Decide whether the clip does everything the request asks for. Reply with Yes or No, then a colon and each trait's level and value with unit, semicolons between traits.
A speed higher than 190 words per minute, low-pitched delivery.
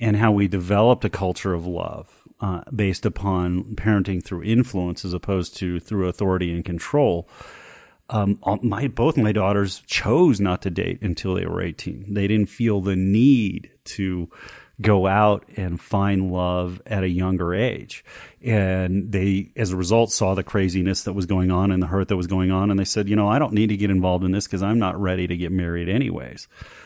Yes: average, 200 wpm; very low, 95 Hz